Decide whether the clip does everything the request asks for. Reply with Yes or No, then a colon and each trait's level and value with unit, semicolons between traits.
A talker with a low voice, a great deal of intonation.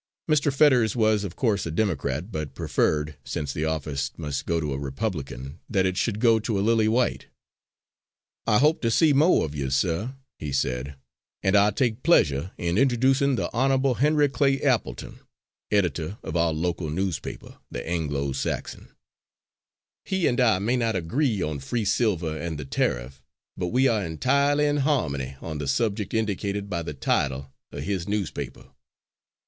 Yes: low, 100 Hz; wide, 8.1 semitones